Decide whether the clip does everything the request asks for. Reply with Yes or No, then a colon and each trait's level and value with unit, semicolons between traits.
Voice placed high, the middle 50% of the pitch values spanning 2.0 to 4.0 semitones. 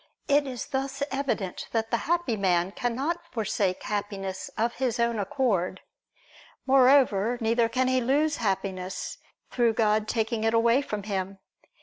No: high, 230 Hz; average, 4.6 semitones